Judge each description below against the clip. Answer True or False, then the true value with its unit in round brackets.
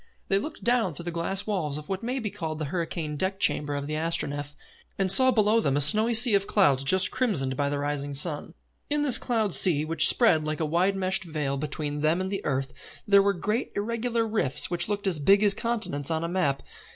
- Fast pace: True (225 wpm)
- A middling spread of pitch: False (5.8 semitones)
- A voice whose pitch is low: False (175 Hz)